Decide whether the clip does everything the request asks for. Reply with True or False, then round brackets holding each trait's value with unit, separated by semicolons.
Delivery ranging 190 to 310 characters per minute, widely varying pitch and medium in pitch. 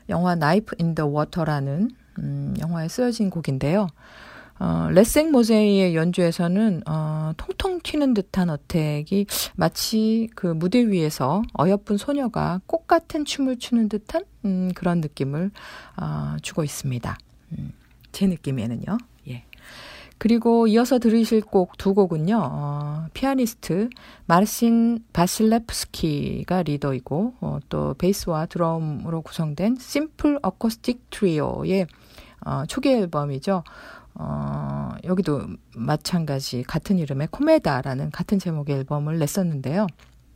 True (270 characters per minute; 7.1 semitones; 180 Hz)